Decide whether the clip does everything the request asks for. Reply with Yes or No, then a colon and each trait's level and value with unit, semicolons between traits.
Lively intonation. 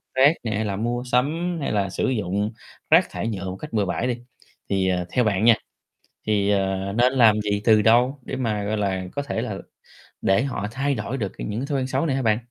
No: average, 4.3 semitones